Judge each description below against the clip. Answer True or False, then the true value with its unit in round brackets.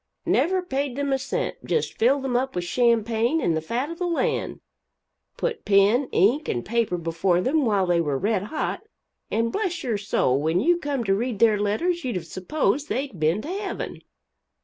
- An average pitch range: False (6.8 semitones)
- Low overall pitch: False (235 Hz)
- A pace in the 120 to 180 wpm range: False (195 wpm)